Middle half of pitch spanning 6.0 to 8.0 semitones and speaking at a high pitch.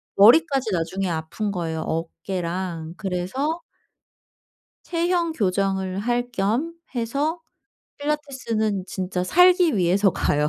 Yes: wide, 7.7 semitones; high, 200 Hz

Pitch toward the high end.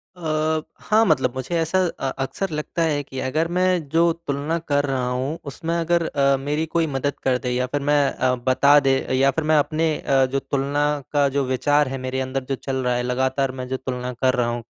No: medium, 140 Hz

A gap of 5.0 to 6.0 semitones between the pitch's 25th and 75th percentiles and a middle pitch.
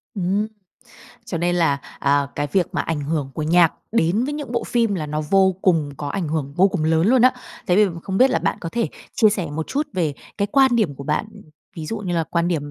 Yes: wide, 5.4 semitones; medium, 175 Hz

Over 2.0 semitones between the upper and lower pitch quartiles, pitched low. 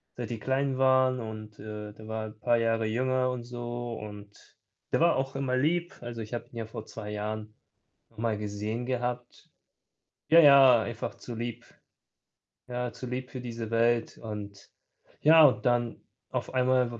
Yes: average, 2.7 semitones; low, 120 Hz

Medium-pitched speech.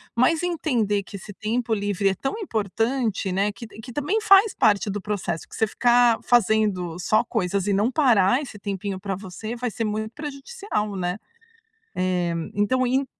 No: high, 215 Hz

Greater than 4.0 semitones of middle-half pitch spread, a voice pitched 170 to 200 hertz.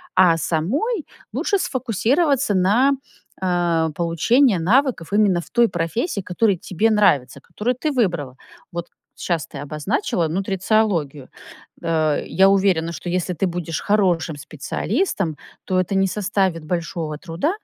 Yes: average, 4.7 semitones; medium, 185 Hz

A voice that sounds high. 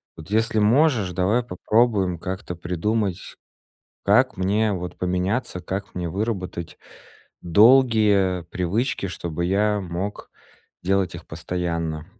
No: very low, 95 Hz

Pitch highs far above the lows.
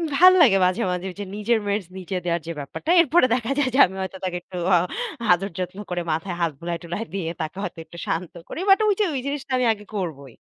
Yes: wide, 6.5 semitones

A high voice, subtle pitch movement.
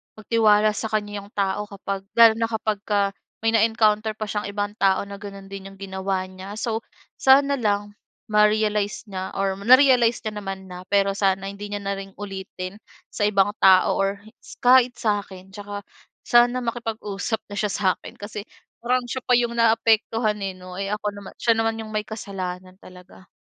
Yes: high, 205 Hz; narrow, 2.2 semitones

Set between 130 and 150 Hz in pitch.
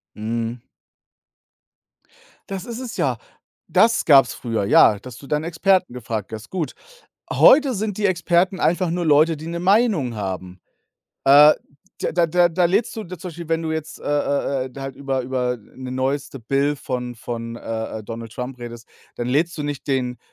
Yes: medium, 140 Hz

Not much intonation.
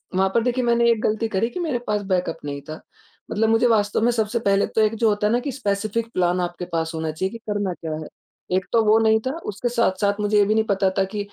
No: average, 3.2 semitones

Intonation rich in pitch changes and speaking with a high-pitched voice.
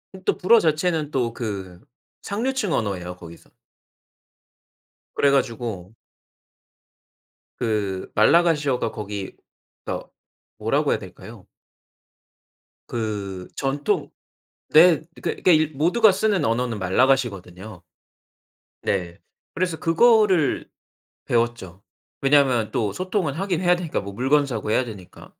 No: wide, 8.2 semitones; low, 130 Hz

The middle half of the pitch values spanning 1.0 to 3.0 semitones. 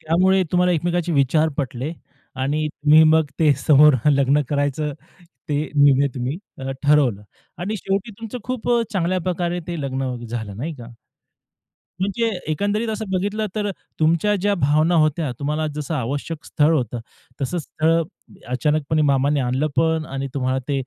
No: average, 4.1 semitones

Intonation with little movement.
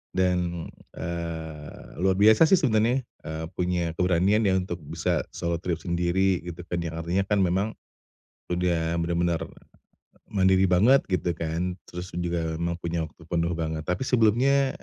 Yes: narrow, 2.3 semitones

